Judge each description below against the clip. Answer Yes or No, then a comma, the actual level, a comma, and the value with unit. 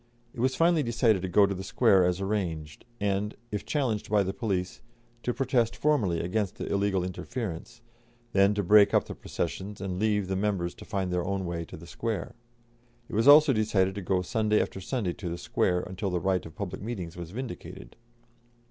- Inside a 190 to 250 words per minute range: Yes, average, 200 wpm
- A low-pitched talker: Yes, low, 100 Hz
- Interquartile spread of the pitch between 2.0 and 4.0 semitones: Yes, average, 3.3 semitones